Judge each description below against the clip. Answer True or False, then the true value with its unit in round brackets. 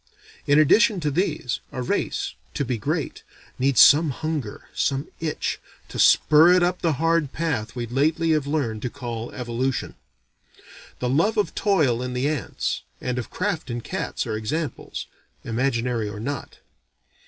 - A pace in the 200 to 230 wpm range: False (155 wpm)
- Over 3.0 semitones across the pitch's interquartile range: True (4.7 semitones)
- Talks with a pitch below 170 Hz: True (140 Hz)